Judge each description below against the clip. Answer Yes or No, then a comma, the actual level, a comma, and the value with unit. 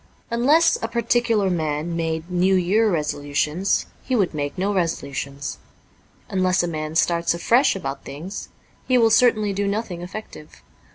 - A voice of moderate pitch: Yes, medium, 180 Hz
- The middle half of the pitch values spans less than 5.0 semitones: No, average, 5.3 semitones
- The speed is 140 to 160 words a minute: Yes, average, 145 wpm